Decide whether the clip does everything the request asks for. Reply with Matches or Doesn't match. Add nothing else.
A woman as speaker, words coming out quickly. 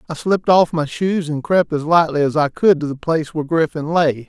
Doesn't match